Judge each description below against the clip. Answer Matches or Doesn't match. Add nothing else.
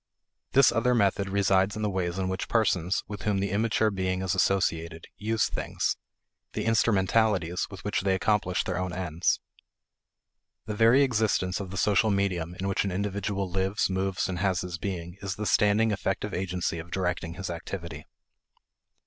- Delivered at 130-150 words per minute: Doesn't match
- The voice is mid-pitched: Doesn't match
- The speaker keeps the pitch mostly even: Matches